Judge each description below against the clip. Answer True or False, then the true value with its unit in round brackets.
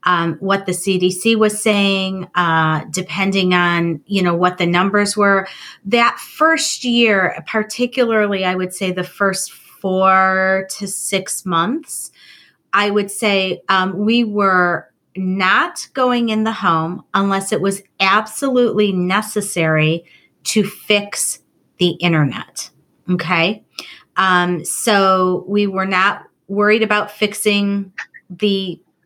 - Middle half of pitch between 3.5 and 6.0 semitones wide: False (2.5 semitones)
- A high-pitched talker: True (195 Hz)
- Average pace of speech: False (120 wpm)